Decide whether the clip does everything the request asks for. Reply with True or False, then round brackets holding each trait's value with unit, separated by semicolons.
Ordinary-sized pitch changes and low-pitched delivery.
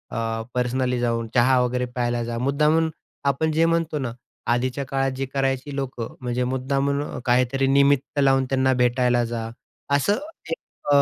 False (2.2 semitones; 130 Hz)